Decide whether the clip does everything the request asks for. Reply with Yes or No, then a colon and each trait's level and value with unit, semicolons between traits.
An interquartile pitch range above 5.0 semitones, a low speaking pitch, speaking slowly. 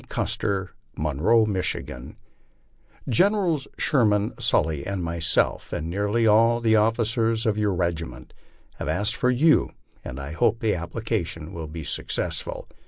Yes: wide, 5.5 semitones; low, 105 Hz; slow, 130 wpm